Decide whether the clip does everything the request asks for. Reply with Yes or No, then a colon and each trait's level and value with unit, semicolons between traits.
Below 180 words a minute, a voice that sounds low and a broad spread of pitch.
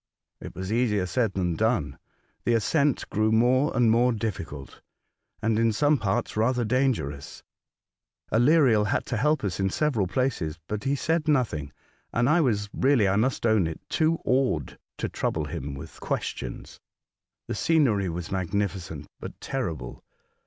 Yes: average, 155 wpm; low, 110 Hz; wide, 5.7 semitones